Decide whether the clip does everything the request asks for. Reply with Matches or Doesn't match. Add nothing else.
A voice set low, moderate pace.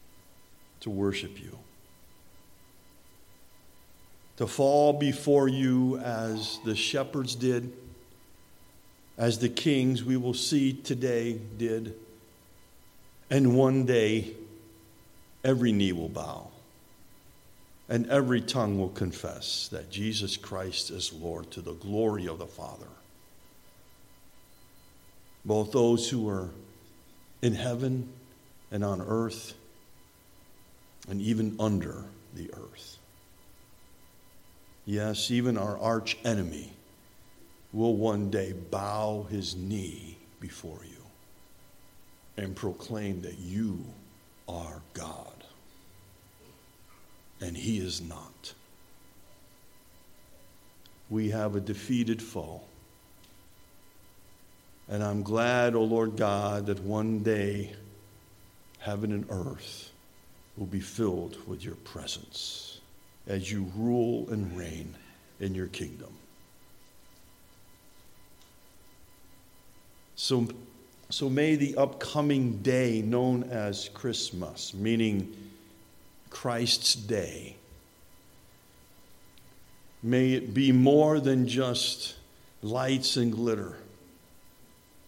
Doesn't match